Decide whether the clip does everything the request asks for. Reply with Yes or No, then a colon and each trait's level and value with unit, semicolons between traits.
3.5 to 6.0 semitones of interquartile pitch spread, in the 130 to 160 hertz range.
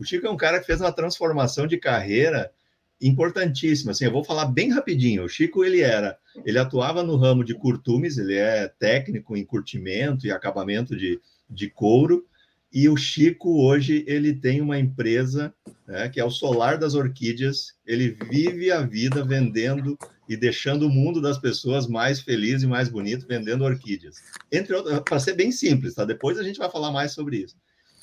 Yes: average, 4.4 semitones; medium, 140 Hz